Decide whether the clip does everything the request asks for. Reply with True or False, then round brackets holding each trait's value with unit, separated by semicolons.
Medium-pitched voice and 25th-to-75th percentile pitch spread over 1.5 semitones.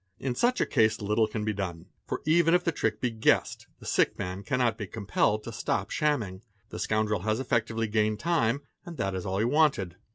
False (110 Hz; 4.1 semitones)